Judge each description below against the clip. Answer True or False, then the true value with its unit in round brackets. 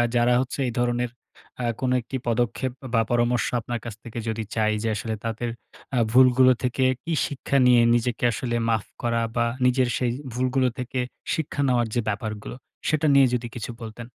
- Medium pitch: False (120 Hz)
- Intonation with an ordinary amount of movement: False (1.7 semitones)